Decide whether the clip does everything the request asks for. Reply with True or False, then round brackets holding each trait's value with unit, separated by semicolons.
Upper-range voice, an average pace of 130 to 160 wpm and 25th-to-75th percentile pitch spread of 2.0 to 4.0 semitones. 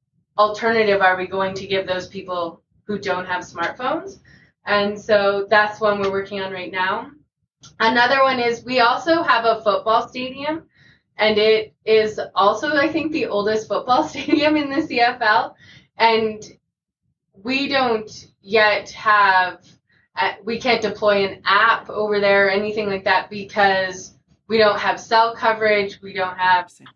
True (210 Hz; 150 wpm; 3.2 semitones)